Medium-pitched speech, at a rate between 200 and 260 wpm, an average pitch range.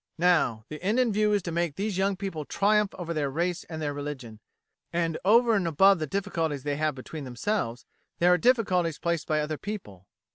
Yes: medium, 170 Hz; fast, 205 wpm; average, 4.9 semitones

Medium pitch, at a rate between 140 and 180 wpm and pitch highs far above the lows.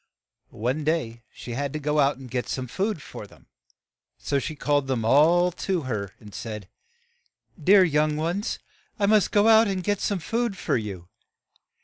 No: medium, 150 Hz; average, 190 wpm; wide, 7.2 semitones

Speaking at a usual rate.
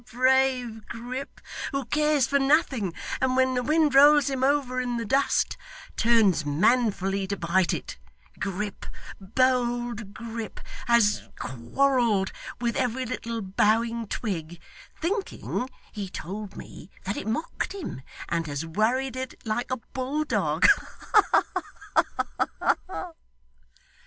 No: slow, 120 wpm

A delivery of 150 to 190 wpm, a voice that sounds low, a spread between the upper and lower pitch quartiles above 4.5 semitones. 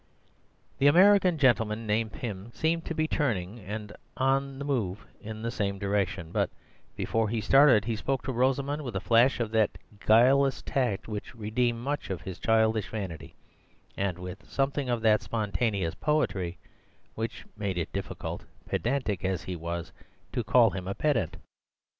Yes: average, 160 wpm; low, 110 Hz; average, 5.2 semitones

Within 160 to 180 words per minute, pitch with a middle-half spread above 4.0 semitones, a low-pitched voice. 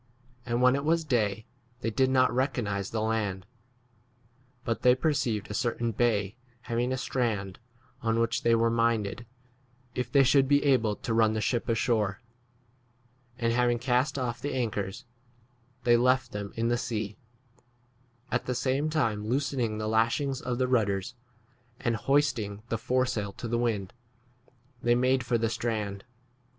No: average, 165 wpm; average, 2.8 semitones; low, 120 Hz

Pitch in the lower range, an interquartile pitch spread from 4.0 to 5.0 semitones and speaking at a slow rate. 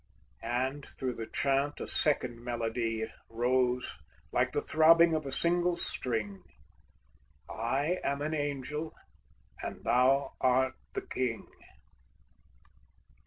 No: low, 130 Hz; average, 3.4 semitones; slow, 110 wpm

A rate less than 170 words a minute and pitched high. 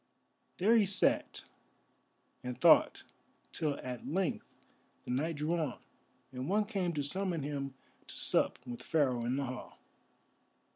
No: average, 140 wpm; medium, 150 Hz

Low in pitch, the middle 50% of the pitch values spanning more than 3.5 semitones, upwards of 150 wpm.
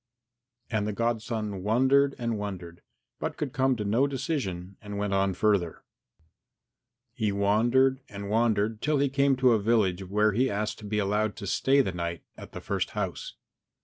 Yes: low, 105 Hz; average, 4.2 semitones; average, 180 wpm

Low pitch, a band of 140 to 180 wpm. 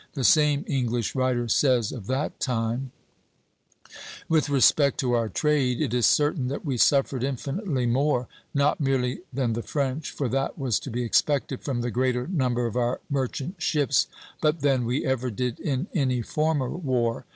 Yes: low, 130 Hz; average, 170 wpm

